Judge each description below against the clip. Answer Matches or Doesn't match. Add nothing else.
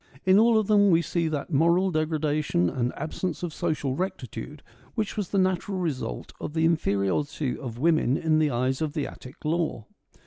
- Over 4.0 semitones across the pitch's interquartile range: Matches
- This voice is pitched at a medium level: Matches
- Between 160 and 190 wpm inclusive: Matches